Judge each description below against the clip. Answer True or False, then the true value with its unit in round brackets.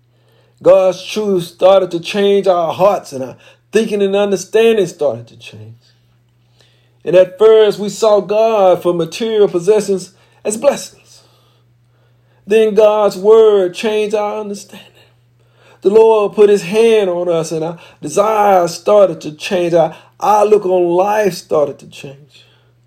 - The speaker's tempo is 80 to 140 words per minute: True (135 wpm)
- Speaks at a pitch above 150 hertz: True (185 Hz)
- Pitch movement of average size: False (8.1 semitones)